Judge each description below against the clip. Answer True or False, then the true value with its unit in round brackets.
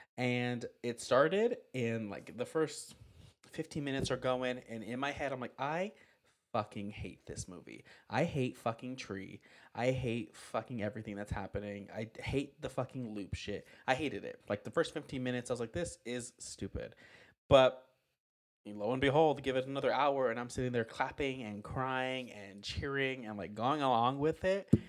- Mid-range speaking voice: False (125 Hz)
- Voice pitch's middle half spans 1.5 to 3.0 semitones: False (3.9 semitones)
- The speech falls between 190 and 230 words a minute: False (180 wpm)